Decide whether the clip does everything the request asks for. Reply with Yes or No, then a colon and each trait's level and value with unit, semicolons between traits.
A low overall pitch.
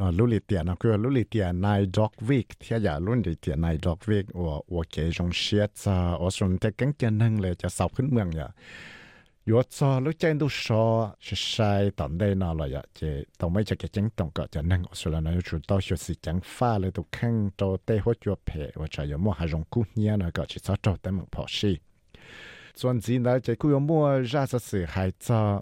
Yes: low, 100 Hz